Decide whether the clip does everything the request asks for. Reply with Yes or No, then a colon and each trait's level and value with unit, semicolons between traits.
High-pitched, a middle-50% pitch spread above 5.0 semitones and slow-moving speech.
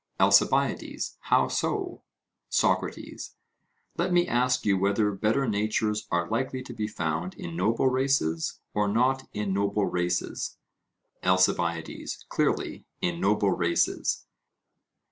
No: low, 105 Hz; wide, 5.6 semitones; slow, 115 wpm